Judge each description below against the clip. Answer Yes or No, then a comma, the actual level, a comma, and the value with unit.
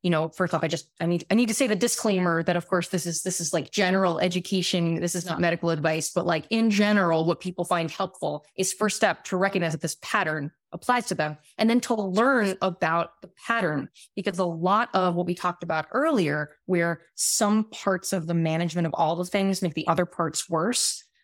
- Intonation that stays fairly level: No, average, 3.1 semitones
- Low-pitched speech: No, medium, 180 Hz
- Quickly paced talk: Yes, fast, 225 wpm